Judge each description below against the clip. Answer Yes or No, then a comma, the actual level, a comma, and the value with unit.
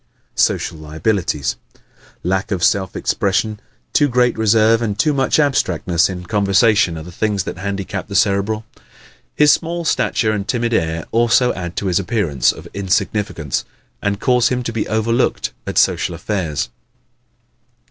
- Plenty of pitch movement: No, average, 4.2 semitones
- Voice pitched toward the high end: No, low, 105 Hz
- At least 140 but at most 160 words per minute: Yes, average, 150 wpm